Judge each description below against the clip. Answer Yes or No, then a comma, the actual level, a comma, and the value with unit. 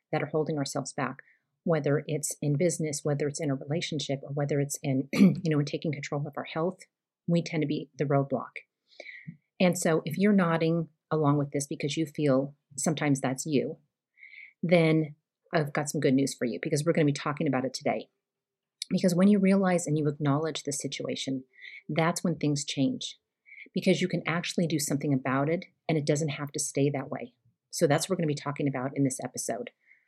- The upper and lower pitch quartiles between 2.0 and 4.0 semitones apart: Yes, average, 2.7 semitones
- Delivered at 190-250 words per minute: Yes, fast, 205 wpm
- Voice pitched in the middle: Yes, medium, 150 Hz